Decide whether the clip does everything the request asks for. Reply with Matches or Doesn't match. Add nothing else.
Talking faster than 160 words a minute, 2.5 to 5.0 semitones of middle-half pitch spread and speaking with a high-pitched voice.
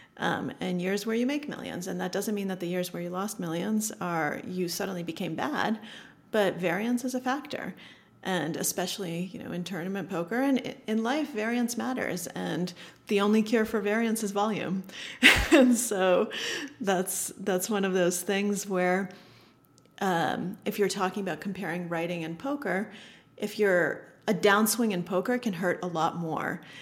Matches